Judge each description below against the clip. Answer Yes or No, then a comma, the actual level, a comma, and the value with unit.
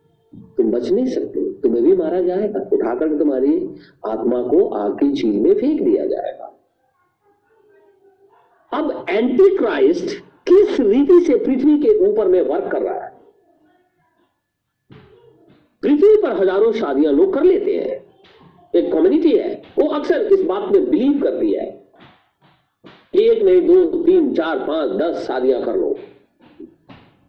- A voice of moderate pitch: No, very high, 370 Hz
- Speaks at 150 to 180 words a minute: No, average, 135 wpm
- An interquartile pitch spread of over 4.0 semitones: No, average, 3.0 semitones